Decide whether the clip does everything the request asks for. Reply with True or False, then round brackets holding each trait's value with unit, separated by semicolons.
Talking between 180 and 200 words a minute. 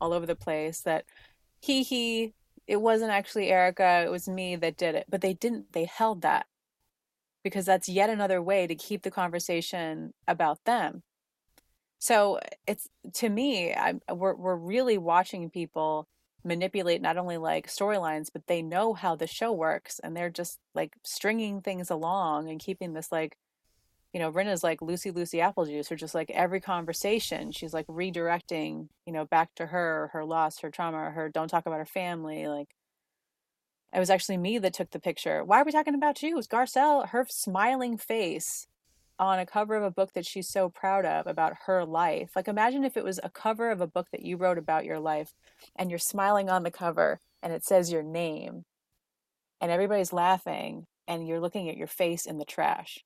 True (195 wpm)